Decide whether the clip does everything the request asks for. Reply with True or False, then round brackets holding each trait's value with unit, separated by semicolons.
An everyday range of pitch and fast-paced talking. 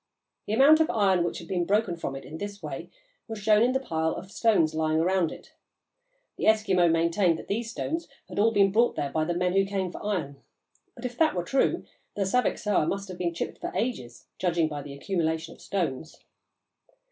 True (4.5 semitones; 210 wpm)